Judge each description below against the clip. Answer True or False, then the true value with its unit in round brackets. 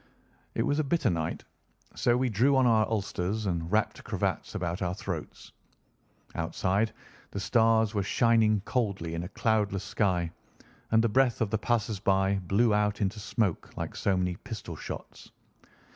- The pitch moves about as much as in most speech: True (3.2 semitones)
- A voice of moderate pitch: False (105 Hz)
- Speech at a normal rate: True (160 wpm)